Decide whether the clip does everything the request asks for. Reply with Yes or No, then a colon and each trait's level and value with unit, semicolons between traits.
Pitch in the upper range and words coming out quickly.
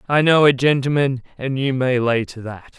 No: low, 135 Hz; fast, 215 wpm